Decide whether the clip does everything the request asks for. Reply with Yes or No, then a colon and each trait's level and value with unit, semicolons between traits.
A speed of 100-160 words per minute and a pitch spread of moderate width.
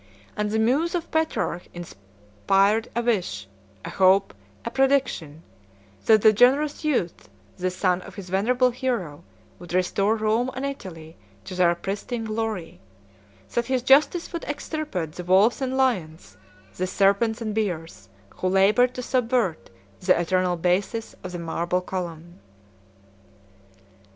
No: slow, 135 wpm; wide, 5.8 semitones